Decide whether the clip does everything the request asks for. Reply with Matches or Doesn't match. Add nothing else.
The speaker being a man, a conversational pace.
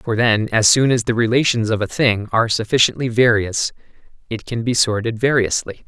Matches